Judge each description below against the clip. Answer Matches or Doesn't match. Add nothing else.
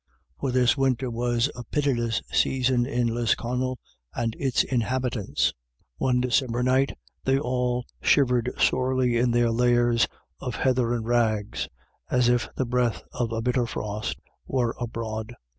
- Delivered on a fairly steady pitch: Matches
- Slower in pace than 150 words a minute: Matches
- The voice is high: Doesn't match